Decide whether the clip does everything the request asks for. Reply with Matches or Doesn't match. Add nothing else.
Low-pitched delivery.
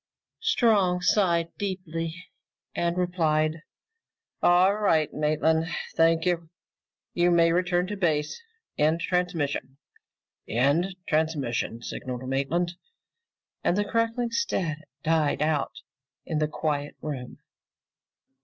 Doesn't match